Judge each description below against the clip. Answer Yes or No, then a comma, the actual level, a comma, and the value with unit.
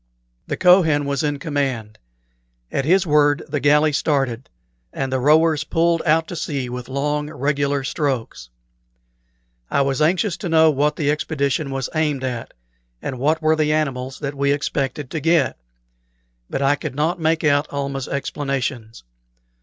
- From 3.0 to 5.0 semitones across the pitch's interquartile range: No, narrow, 2.4 semitones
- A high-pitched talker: No, medium, 145 Hz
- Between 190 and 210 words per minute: No, average, 155 wpm